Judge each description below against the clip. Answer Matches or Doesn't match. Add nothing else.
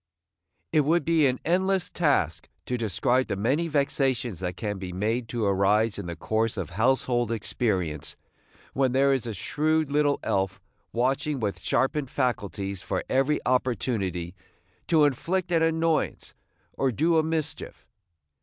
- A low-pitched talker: Matches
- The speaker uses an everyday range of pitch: Doesn't match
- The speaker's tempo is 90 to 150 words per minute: Matches